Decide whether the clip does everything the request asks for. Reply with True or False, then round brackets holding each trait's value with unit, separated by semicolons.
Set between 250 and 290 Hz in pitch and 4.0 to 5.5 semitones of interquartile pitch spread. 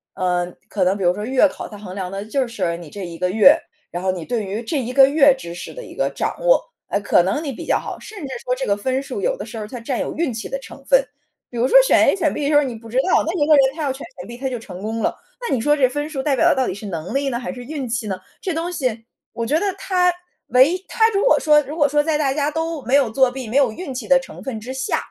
True (260 Hz; 5.2 semitones)